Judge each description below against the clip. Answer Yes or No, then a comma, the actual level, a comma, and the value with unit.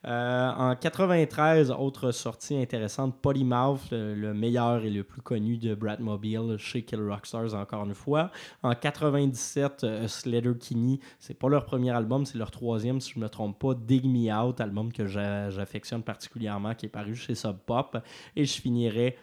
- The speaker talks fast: No, average, 185 wpm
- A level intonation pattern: No, average, 3.4 semitones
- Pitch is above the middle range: No, low, 120 Hz